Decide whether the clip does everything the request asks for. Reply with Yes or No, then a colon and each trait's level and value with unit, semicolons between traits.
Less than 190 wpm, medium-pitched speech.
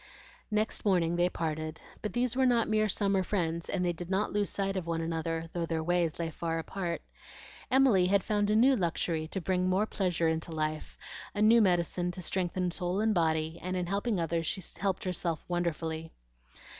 No: average, 195 wpm; medium, 180 Hz